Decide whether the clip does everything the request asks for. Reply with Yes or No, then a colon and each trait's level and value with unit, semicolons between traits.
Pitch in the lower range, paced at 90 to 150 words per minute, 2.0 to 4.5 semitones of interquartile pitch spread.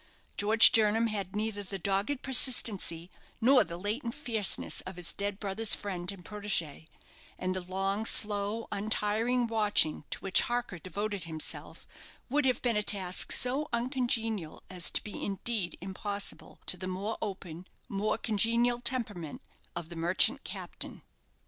No: high, 205 Hz; average, 145 wpm; average, 3.5 semitones